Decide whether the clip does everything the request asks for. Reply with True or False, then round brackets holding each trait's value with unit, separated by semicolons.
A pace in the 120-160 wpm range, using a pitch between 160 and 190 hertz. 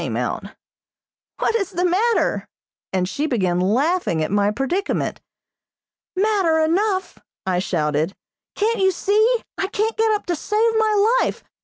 False (145 wpm; 370 Hz)